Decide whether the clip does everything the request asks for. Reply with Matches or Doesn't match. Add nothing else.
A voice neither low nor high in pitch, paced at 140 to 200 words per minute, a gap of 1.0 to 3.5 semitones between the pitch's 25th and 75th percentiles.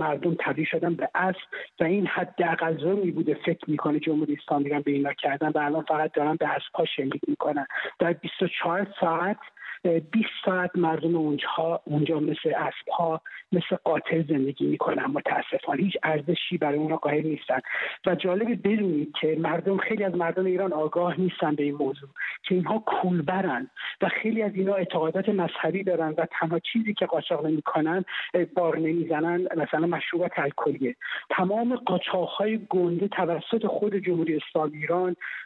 Matches